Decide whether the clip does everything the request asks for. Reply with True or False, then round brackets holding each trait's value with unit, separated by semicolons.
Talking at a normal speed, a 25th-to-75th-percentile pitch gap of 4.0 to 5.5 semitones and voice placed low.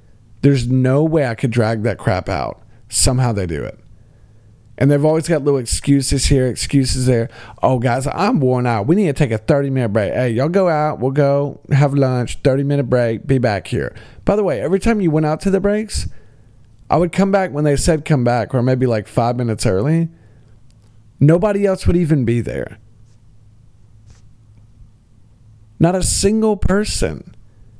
True (185 wpm; 4.9 semitones; 125 Hz)